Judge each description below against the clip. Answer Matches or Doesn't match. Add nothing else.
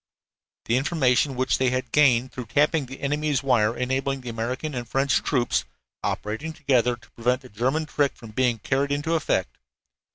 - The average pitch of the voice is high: Doesn't match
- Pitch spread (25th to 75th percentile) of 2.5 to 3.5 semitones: Matches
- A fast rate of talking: Doesn't match